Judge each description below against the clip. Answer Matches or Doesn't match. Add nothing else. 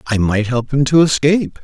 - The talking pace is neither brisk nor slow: Doesn't match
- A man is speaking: Matches